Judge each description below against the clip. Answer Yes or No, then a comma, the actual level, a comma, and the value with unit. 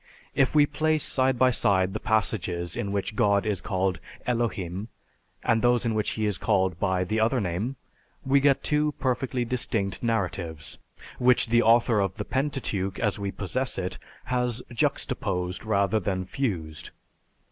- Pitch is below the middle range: Yes, low, 110 Hz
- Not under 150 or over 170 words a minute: Yes, average, 160 wpm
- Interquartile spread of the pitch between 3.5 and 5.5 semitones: Yes, average, 4.8 semitones